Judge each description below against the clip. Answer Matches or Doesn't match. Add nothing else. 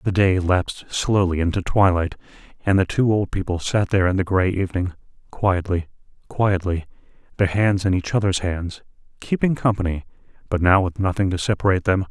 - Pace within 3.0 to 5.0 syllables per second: Doesn't match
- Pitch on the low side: Matches